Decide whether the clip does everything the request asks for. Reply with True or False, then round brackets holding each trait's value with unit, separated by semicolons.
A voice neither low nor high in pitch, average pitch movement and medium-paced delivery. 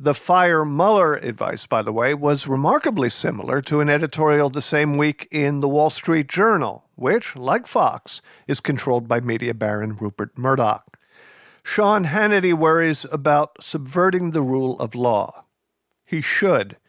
True (150 Hz; 3.9 semitones; 150 wpm)